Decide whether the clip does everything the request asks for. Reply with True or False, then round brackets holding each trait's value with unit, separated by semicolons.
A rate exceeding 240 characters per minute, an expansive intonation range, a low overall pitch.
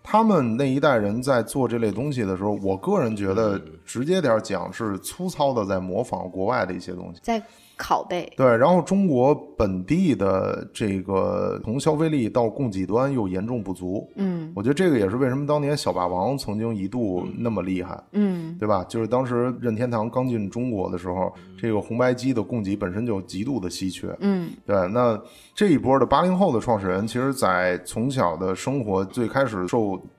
True (290 characters per minute; 6.3 semitones; 115 Hz)